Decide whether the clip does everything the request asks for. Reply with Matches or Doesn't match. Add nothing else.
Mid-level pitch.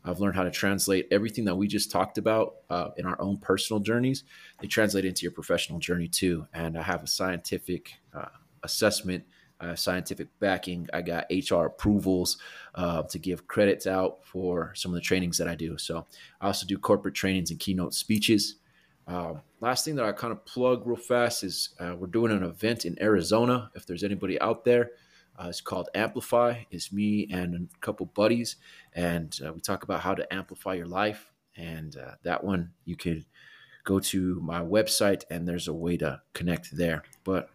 Doesn't match